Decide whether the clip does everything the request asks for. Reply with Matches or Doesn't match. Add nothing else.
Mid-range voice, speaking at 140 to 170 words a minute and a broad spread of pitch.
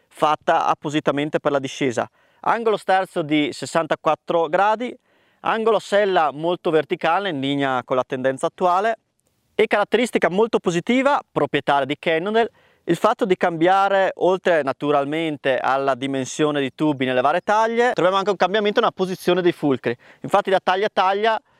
Matches